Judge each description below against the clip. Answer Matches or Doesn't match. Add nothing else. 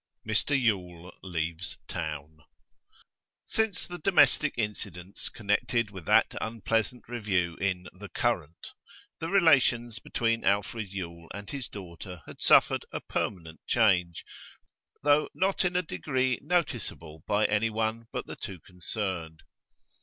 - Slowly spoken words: Matches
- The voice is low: Matches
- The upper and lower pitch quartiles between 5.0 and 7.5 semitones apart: Matches